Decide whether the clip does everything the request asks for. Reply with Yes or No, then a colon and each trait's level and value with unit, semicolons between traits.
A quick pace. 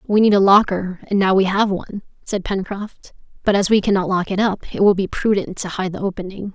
Yes: fast, 240 wpm